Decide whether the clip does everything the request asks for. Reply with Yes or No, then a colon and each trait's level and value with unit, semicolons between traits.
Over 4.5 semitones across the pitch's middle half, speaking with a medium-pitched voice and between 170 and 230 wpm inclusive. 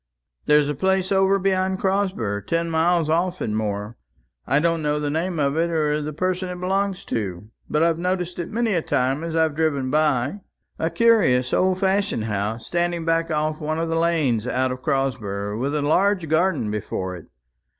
Yes: wide, 5.6 semitones; medium, 160 Hz; average, 190 wpm